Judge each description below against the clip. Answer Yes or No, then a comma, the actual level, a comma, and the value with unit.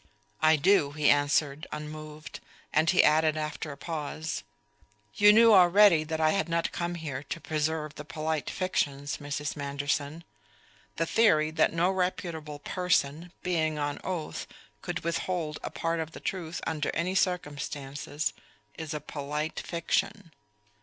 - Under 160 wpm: Yes, average, 145 wpm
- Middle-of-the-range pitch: Yes, medium, 155 Hz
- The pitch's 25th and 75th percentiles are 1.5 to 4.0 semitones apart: Yes, narrow, 2.4 semitones